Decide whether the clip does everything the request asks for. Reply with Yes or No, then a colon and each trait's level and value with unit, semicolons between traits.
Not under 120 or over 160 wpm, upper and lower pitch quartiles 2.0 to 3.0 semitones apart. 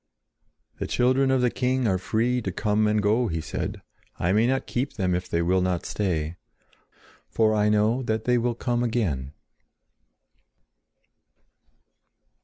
No: average, 150 wpm; average, 4.9 semitones